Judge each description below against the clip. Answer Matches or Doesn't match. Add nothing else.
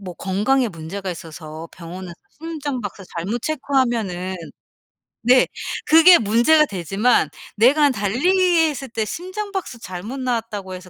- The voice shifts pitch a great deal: Matches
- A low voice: Doesn't match